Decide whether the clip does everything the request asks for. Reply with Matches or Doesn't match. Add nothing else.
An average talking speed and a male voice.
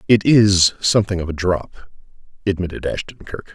Matches